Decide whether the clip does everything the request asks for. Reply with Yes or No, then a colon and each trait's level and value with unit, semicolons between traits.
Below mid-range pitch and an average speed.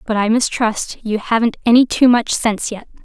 No: high, 225 Hz; average, 195 wpm